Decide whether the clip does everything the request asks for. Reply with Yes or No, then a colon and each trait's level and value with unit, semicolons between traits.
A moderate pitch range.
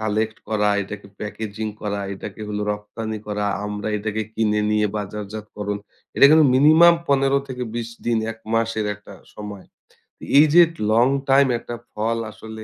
No: narrow, 2.3 semitones